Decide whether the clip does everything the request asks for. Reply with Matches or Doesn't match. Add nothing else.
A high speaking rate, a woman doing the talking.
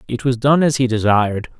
Doesn't match